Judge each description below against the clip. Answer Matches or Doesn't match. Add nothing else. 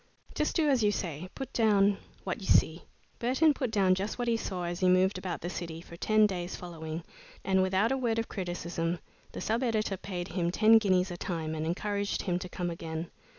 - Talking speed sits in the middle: Doesn't match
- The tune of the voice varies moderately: Matches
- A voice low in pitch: Doesn't match